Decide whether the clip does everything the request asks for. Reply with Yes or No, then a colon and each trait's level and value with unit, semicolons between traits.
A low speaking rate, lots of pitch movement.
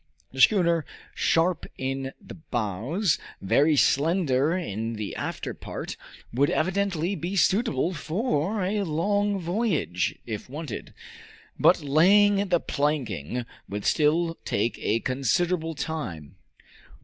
Yes: slow, 115 wpm; wide, 6.1 semitones